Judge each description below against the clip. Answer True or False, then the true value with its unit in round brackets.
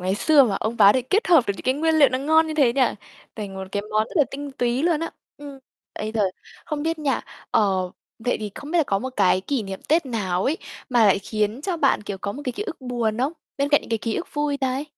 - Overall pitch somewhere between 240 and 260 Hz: True (255 Hz)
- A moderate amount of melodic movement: False (5.7 semitones)